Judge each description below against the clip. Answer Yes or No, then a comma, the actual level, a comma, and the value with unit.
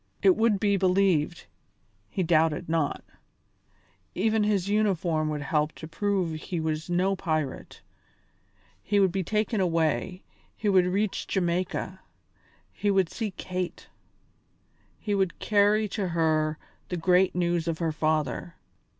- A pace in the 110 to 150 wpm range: Yes, slow, 135 wpm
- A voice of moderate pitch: Yes, medium, 180 Hz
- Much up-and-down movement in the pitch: No, average, 3.6 semitones